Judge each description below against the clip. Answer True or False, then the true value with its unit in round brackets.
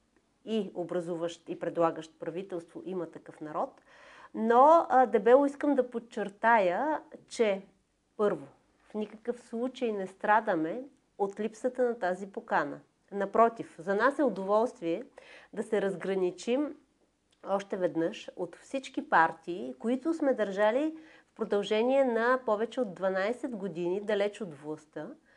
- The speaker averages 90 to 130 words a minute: True (120 wpm)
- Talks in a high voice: True (215 Hz)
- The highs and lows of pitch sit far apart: True (6.0 semitones)